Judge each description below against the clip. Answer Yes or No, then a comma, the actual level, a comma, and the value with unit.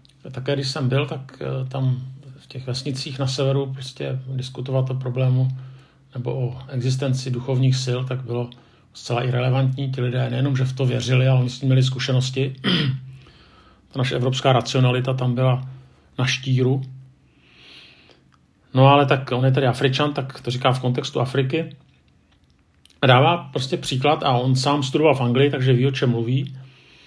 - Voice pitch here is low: Yes, low, 130 Hz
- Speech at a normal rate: Yes, average, 160 wpm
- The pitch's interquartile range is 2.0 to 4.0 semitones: No, narrow, 1.3 semitones